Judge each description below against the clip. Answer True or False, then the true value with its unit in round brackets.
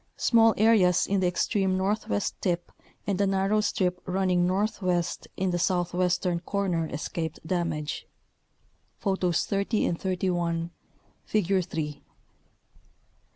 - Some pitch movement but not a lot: False (2.2 semitones)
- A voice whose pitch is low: False (180 Hz)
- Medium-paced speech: False (115 wpm)